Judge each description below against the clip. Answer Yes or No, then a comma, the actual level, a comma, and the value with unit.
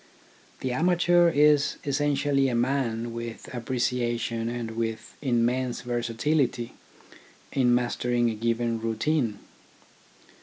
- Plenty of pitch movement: No, average, 2.9 semitones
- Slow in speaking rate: Yes, slow, 105 wpm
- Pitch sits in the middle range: No, low, 120 Hz